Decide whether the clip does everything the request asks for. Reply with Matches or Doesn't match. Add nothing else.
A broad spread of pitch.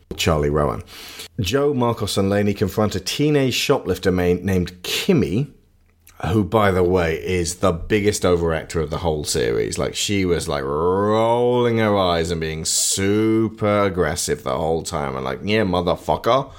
Doesn't match